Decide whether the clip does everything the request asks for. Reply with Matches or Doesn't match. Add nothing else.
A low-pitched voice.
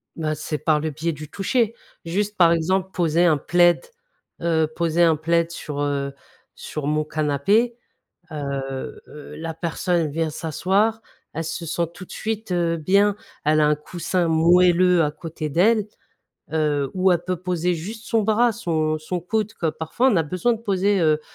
Doesn't match